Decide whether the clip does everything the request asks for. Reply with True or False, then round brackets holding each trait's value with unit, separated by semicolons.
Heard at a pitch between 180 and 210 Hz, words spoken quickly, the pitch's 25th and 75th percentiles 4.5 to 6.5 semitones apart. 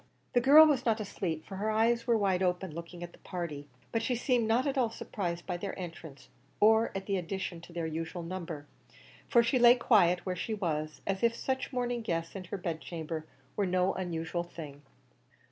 True (185 Hz; 210 wpm; 5.2 semitones)